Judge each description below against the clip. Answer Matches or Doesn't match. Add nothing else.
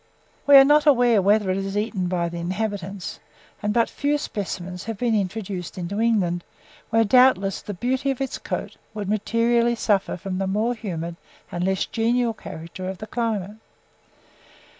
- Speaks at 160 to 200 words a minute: Matches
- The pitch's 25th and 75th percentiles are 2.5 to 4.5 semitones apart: Matches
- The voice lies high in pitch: Matches